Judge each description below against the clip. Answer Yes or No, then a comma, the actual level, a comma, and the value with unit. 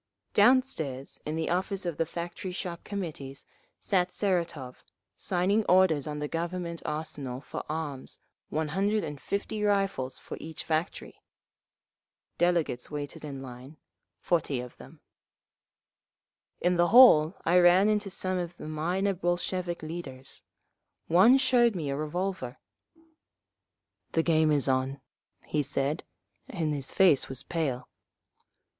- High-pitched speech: No, medium, 165 Hz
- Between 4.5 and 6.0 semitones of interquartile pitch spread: No, average, 4.1 semitones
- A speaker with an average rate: No, slow, 125 wpm